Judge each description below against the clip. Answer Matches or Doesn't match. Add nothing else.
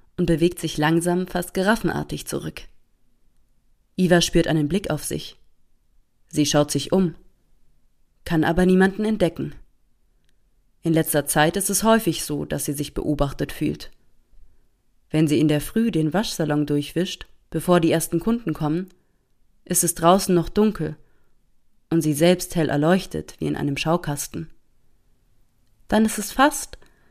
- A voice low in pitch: Doesn't match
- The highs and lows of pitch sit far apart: Doesn't match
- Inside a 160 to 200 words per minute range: Doesn't match